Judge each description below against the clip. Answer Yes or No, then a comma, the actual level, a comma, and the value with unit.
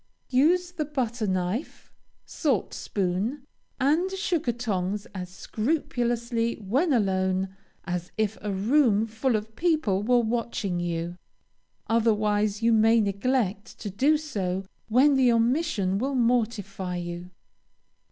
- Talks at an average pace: No, slow, 120 wpm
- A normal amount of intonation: Yes, average, 5.0 semitones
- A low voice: No, high, 225 Hz